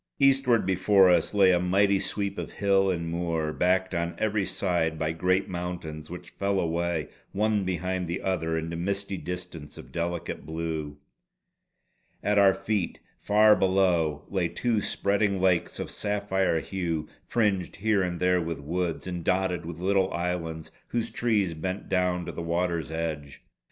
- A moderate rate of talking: Yes, average, 155 wpm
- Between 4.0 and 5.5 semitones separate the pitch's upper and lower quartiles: No, average, 2.8 semitones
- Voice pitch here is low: Yes, very low, 90 Hz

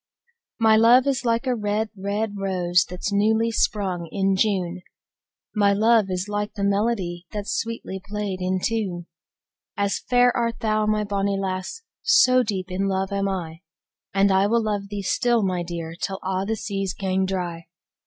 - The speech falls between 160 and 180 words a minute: Yes, average, 175 wpm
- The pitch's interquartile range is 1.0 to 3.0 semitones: Yes, narrow, 2.6 semitones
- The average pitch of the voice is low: No, high, 200 Hz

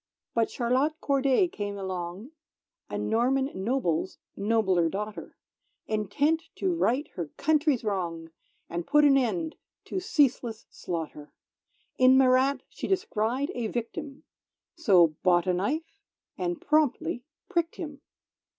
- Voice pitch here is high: Yes, high, 245 Hz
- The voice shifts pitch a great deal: Yes, wide, 7.2 semitones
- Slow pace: Yes, slow, 125 wpm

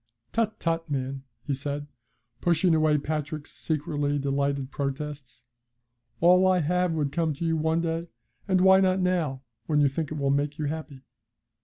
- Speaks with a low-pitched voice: No, medium, 150 Hz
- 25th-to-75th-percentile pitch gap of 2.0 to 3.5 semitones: Yes, average, 3.0 semitones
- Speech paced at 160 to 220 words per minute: Yes, average, 165 wpm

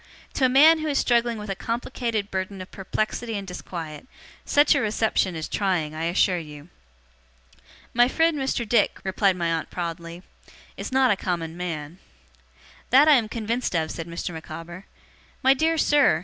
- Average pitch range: No, wide, 6.5 semitones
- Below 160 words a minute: No, average, 170 wpm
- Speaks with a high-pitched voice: Yes, high, 195 Hz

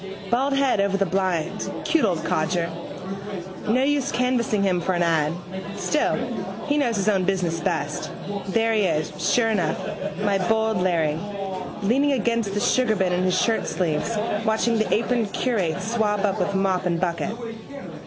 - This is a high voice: Yes, high, 200 Hz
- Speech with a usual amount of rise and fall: Yes, average, 4.2 semitones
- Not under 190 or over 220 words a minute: No, average, 155 wpm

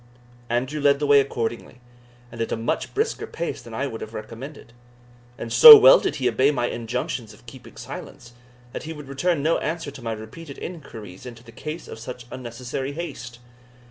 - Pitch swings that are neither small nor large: Yes, average, 4.4 semitones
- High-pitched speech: No, low, 130 Hz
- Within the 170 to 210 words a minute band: Yes, average, 190 wpm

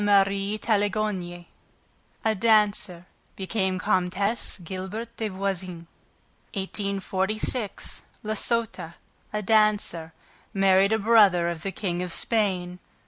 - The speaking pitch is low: No, high, 195 Hz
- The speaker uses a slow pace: Yes, slow, 100 wpm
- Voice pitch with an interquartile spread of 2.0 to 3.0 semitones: Yes, narrow, 2.6 semitones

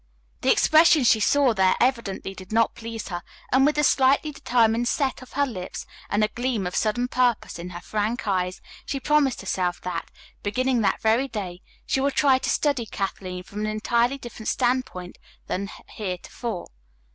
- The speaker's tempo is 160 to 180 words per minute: Yes, average, 175 wpm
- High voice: Yes, high, 230 Hz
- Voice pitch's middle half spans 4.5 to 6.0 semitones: Yes, average, 5.1 semitones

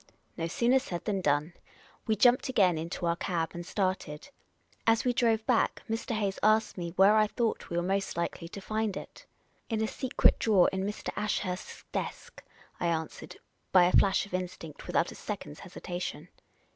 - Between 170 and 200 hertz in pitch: Yes, high, 190 Hz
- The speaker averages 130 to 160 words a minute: No, average, 185 wpm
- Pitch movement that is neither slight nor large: Yes, average, 4.1 semitones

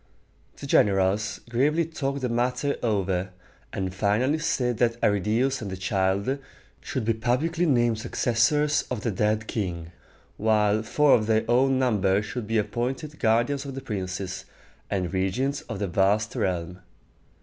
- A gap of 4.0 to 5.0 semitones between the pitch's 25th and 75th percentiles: Yes, average, 4.7 semitones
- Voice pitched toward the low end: Yes, low, 110 Hz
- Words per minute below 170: Yes, average, 150 wpm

